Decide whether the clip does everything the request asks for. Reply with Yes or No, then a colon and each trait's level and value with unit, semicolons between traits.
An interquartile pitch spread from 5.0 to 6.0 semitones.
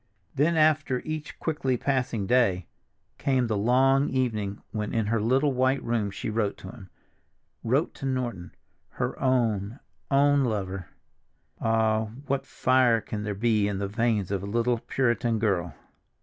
No: average, 4.0 semitones